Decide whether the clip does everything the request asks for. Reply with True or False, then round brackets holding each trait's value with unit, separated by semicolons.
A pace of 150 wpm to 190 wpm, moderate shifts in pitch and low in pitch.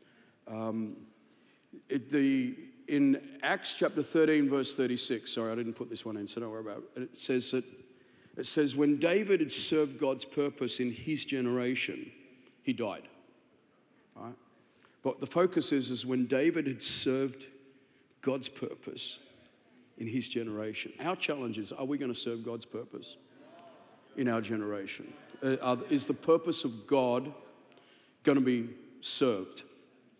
True (155 wpm; 3.5 semitones; 130 Hz)